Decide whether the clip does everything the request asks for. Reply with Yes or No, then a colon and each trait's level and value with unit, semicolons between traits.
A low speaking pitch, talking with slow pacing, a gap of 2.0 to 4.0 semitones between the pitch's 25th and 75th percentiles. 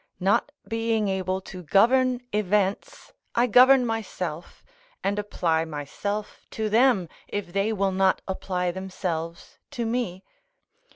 No: high, 200 Hz; slow, 120 wpm; average, 3.6 semitones